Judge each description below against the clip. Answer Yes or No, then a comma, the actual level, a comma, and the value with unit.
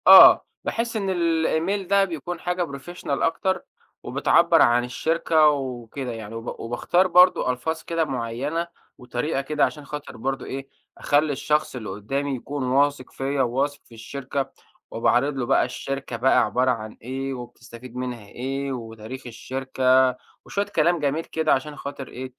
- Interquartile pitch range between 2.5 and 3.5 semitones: No, average, 4.0 semitones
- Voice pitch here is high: No, low, 135 Hz